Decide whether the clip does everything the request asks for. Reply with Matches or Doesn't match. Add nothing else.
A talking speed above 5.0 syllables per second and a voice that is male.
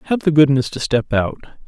Matches